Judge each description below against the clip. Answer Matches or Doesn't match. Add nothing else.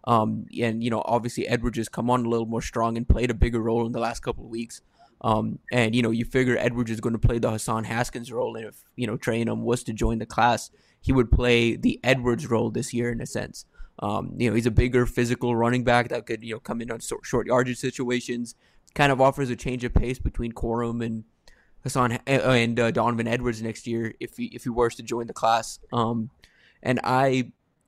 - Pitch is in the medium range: Doesn't match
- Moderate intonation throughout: Doesn't match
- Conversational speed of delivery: Doesn't match